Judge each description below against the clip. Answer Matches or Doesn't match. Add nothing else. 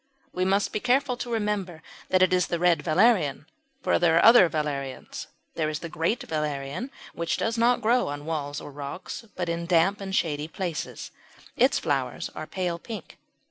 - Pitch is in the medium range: Matches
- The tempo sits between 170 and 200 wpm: Matches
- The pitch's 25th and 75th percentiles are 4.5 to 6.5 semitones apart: Matches